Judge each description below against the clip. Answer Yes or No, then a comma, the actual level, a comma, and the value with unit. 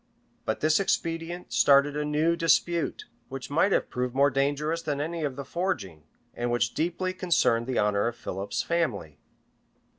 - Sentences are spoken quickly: No, average, 160 wpm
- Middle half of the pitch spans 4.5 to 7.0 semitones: Yes, wide, 5.5 semitones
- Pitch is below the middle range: No, medium, 145 Hz